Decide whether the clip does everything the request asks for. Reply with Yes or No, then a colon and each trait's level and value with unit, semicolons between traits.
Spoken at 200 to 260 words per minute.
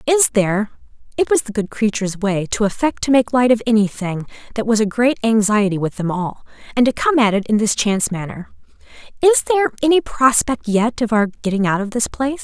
Yes: fast, 205 wpm